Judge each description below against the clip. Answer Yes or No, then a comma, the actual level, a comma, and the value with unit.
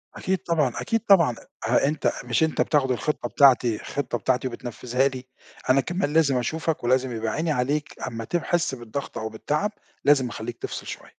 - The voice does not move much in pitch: No, average, 4.3 semitones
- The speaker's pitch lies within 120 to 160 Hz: Yes, low, 135 Hz